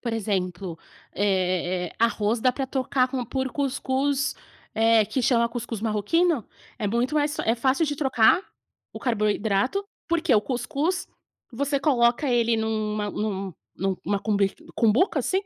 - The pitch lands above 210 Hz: Yes, high, 235 Hz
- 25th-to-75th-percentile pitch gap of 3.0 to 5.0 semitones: Yes, average, 4.5 semitones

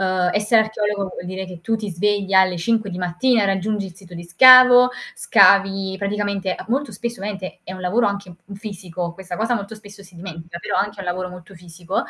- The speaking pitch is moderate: No, high, 195 Hz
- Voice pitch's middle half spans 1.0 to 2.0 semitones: No, narrow, 2.5 semitones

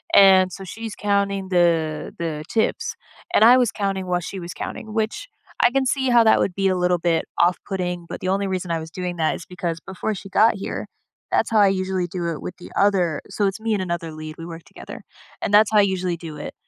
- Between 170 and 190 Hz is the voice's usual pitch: Yes, medium, 185 Hz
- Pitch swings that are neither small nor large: Yes, average, 3.0 semitones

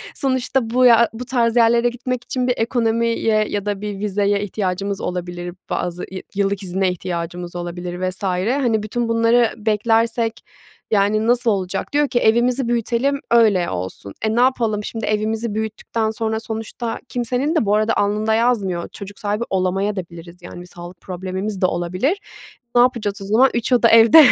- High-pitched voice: Yes, high, 215 Hz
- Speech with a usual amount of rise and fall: Yes, average, 3.7 semitones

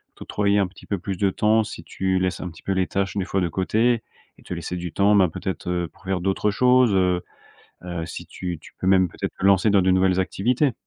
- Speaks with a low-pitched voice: Yes, very low, 95 Hz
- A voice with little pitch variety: Yes, narrow, 2.0 semitones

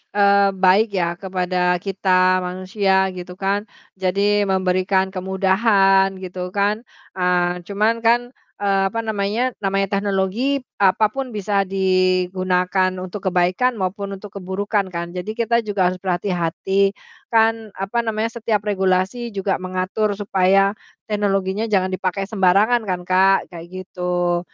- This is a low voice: No, high, 195 Hz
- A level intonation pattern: Yes, narrow, 1.9 semitones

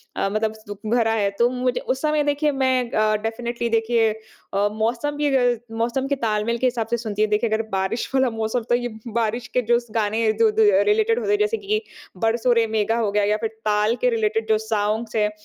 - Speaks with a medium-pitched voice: No, high, 230 Hz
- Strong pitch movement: No, average, 2.9 semitones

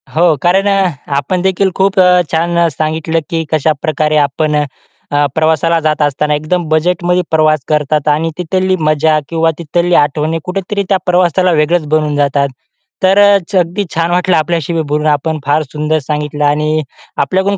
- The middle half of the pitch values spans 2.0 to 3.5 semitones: Yes, average, 2.8 semitones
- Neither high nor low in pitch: Yes, medium, 160 Hz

